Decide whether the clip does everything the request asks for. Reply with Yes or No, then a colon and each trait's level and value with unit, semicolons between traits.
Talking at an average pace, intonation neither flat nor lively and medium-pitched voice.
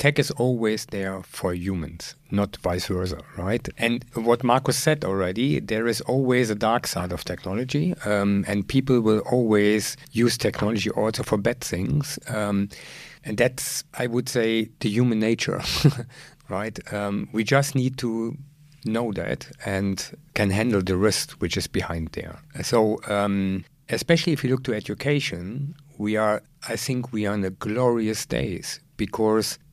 No: average, 160 wpm; average, 4.2 semitones; low, 115 Hz